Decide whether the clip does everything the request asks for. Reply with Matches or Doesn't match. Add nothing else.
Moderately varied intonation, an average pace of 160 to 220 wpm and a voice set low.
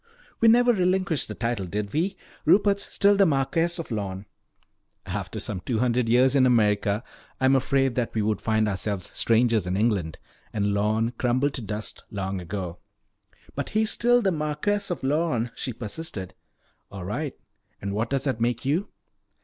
Doesn't match